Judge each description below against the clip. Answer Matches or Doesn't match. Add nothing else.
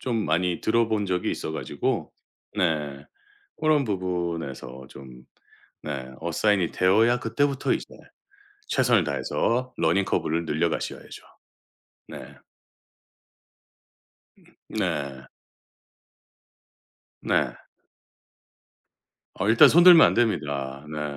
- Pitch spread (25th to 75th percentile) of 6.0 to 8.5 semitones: Matches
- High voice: Doesn't match